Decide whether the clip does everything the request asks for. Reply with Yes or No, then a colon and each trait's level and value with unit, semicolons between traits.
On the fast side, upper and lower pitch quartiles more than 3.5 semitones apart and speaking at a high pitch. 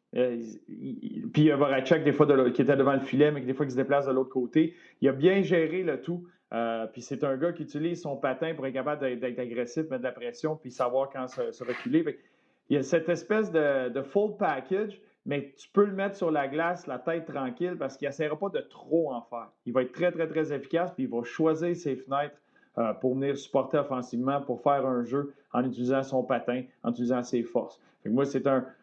No: fast, 235 wpm; average, 4.3 semitones; medium, 140 Hz